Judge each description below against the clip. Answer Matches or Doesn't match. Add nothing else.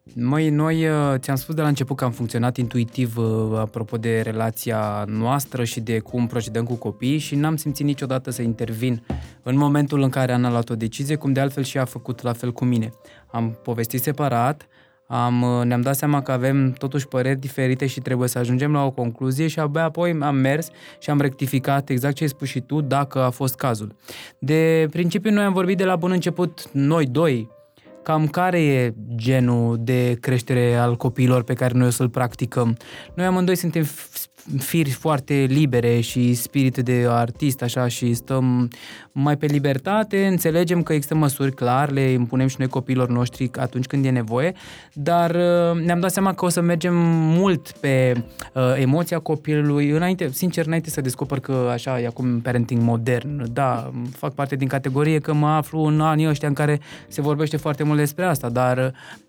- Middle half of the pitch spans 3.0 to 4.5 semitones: Matches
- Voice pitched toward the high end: Doesn't match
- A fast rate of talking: Matches